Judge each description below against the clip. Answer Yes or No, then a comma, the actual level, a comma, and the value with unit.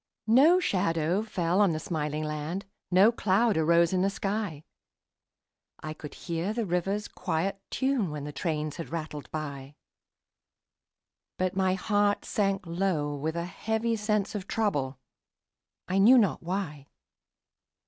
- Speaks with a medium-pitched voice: Yes, medium, 180 Hz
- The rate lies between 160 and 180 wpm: No, average, 140 wpm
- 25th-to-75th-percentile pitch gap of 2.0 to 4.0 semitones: No, average, 4.7 semitones